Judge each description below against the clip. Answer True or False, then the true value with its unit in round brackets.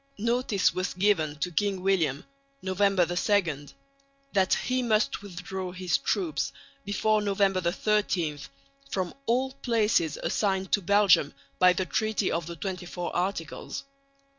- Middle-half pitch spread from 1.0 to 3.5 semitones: True (2.9 semitones)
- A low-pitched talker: False (190 Hz)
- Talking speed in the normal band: False (125 wpm)